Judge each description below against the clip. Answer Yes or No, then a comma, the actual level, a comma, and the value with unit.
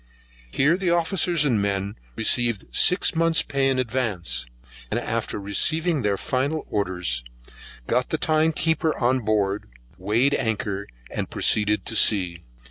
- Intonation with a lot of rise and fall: Yes, wide, 7.4 semitones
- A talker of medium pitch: No, low, 120 Hz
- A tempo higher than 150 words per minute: No, slow, 135 wpm